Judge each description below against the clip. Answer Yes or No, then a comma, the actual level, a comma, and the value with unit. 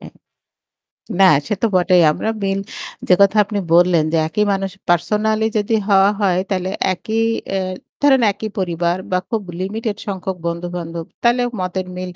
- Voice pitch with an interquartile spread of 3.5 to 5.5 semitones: No, average, 3.0 semitones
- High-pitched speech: Yes, high, 195 Hz